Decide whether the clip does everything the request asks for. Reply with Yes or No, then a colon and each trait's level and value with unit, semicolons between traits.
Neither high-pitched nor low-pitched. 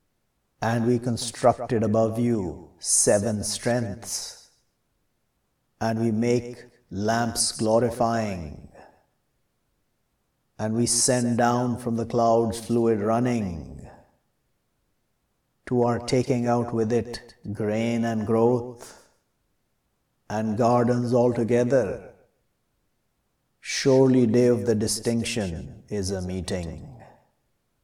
No: low, 115 Hz